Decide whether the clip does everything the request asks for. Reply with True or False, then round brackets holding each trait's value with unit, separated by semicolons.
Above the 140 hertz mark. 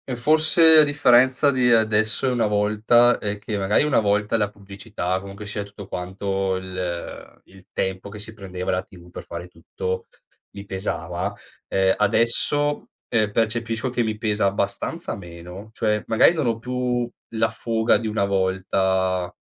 False (105 Hz)